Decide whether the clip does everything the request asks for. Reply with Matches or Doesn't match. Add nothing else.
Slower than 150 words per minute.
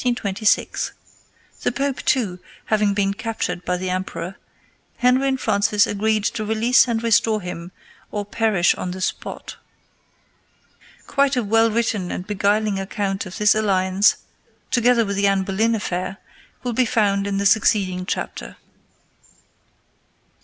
Matches